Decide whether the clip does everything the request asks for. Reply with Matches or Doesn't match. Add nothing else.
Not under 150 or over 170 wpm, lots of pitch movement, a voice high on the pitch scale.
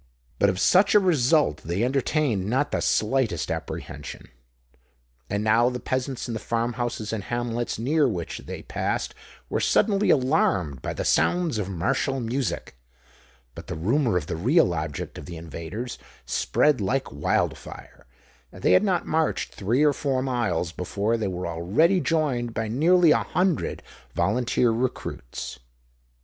Doesn't match